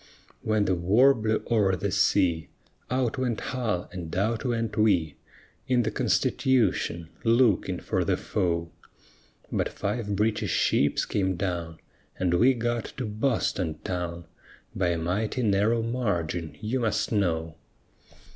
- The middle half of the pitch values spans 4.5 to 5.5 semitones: Yes, average, 4.8 semitones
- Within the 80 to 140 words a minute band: Yes, slow, 135 wpm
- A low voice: Yes, low, 105 Hz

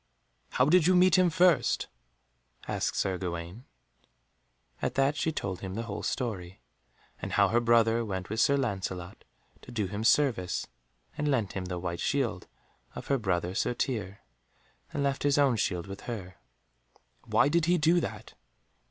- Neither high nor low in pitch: No, low, 115 Hz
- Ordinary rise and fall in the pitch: No, wide, 7.0 semitones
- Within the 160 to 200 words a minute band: Yes, average, 165 wpm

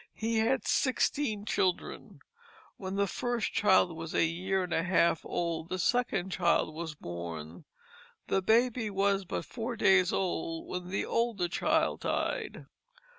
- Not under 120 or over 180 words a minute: Yes, average, 145 wpm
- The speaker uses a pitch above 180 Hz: Yes, high, 190 Hz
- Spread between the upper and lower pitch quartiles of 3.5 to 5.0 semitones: Yes, average, 4.6 semitones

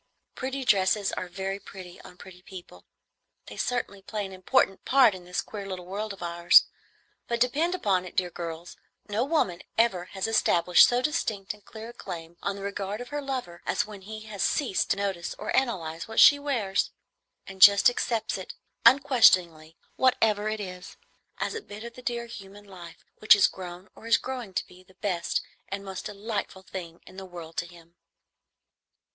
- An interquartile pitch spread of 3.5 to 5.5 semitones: Yes, average, 3.8 semitones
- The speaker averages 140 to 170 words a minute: No, average, 185 wpm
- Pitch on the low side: No, high, 195 Hz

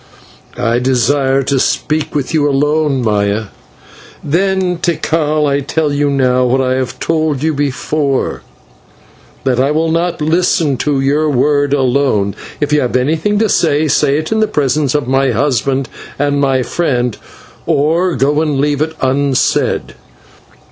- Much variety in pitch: No, average, 2.8 semitones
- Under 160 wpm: Yes, average, 150 wpm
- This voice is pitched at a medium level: Yes, medium, 145 Hz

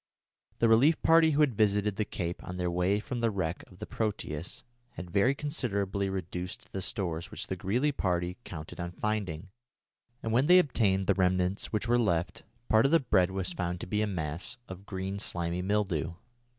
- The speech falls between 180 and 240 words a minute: Yes, average, 190 wpm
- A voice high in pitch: No, very low, 95 Hz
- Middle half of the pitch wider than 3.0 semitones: Yes, average, 3.8 semitones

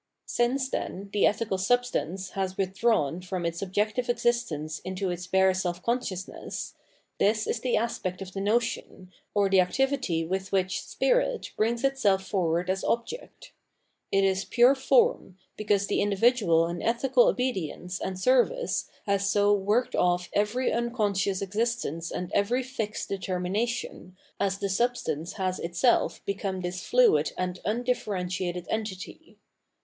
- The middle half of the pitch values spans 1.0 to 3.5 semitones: No, average, 4.4 semitones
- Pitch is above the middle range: Yes, high, 200 Hz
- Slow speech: No, average, 145 wpm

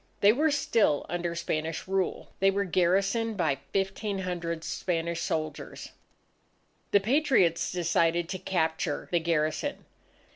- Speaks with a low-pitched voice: No, medium, 175 Hz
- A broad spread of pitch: No, average, 3.1 semitones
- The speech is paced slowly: Yes, slow, 115 wpm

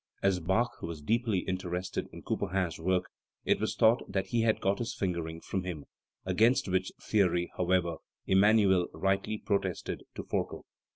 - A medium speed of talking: Yes, average, 155 wpm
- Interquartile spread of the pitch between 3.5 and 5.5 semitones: No, narrow, 2.5 semitones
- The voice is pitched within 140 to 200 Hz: No, very low, 95 Hz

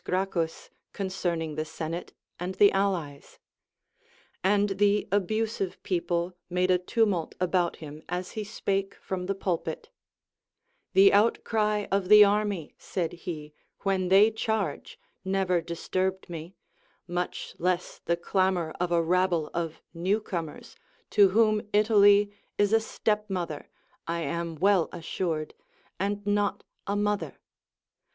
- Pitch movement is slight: No, average, 3.1 semitones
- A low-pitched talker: No, medium, 185 Hz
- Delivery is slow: Yes, slow, 130 wpm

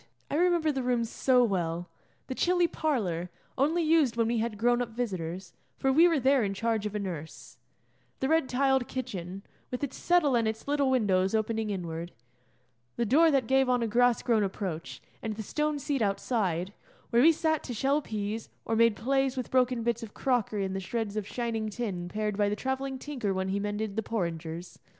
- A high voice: Yes, high, 230 Hz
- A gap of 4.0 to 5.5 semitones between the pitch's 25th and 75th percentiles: Yes, average, 4.9 semitones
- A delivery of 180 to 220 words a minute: Yes, average, 200 wpm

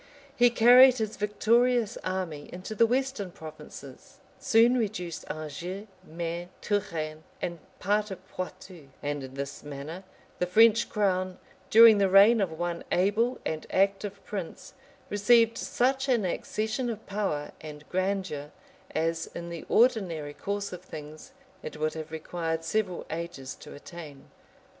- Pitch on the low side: No, medium, 185 Hz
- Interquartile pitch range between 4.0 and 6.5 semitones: Yes, average, 5.1 semitones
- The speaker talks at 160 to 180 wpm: No, average, 140 wpm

